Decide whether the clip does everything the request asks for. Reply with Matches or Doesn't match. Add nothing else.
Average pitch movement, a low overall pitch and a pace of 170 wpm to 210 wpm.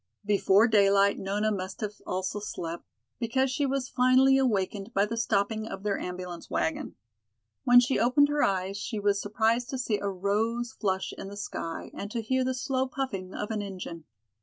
Doesn't match